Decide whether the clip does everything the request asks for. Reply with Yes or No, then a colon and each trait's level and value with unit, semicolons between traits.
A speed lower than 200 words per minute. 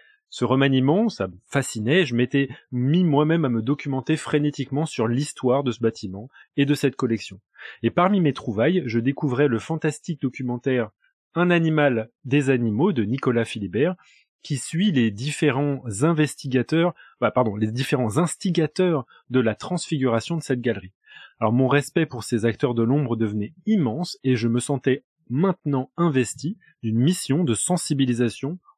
Yes: average, 155 wpm